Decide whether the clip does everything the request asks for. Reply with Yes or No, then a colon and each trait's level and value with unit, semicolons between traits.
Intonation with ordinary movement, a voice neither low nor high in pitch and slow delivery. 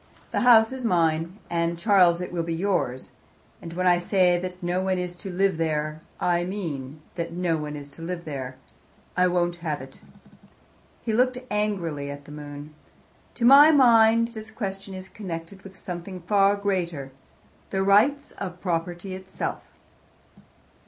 No: average, 3.3 semitones; medium, 180 Hz; average, 160 wpm